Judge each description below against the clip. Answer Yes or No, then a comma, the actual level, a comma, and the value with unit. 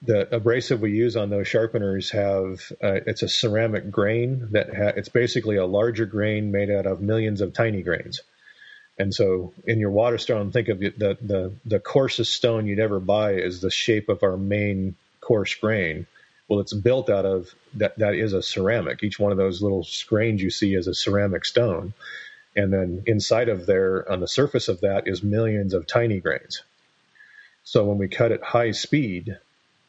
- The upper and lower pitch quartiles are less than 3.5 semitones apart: Yes, narrow, 2.6 semitones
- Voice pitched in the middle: No, low, 105 Hz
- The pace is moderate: Yes, average, 190 wpm